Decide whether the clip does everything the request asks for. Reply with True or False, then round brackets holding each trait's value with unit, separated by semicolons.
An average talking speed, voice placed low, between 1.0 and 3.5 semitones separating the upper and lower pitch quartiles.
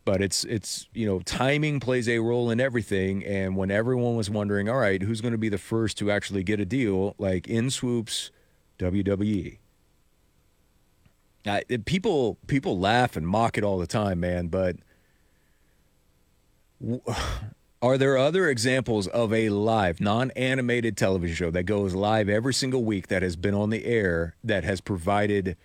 False (165 wpm; 105 Hz; 4.0 semitones)